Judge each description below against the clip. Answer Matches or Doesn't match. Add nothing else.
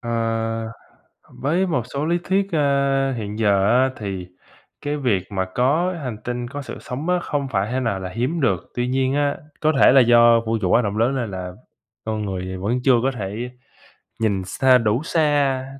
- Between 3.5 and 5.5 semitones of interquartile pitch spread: Matches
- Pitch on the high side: Doesn't match